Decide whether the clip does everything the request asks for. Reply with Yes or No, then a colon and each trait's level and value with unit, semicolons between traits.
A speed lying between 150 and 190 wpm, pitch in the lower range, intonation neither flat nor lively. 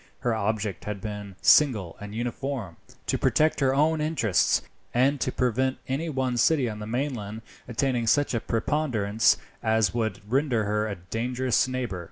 Yes: average, 160 wpm; low, 120 Hz; average, 3.9 semitones